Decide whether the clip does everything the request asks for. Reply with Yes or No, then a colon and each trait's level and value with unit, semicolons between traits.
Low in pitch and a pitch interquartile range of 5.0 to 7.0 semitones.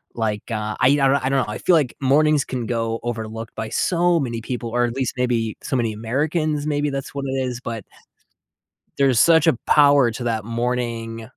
No: low, 125 Hz; average, 3.7 semitones